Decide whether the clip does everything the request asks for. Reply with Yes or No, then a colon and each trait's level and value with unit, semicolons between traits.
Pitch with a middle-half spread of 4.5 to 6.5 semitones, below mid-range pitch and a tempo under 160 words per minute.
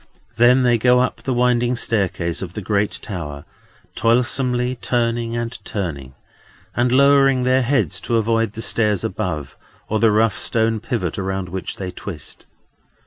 No: average, 4.0 semitones; low, 115 Hz; average, 150 wpm